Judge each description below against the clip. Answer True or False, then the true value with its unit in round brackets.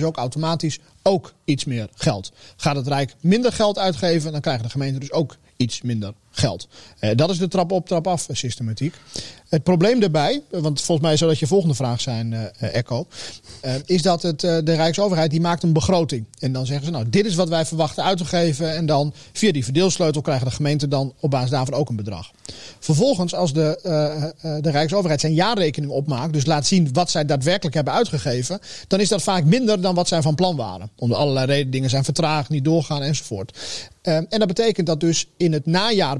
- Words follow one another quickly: True (205 wpm)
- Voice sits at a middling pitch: True (155 Hz)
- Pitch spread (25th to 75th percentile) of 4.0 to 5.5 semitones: True (4.4 semitones)